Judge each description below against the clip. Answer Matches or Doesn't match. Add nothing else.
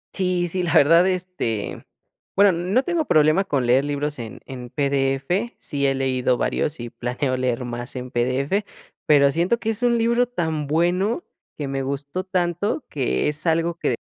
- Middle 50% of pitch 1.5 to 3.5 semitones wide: Doesn't match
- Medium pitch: Matches